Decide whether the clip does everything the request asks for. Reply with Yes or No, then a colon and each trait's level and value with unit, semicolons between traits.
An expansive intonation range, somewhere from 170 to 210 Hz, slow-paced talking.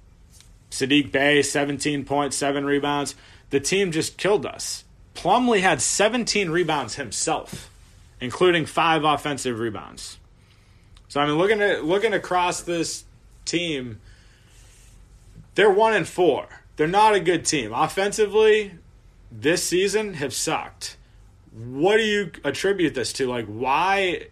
No: wide, 8.1 semitones; medium, 145 Hz; slow, 125 wpm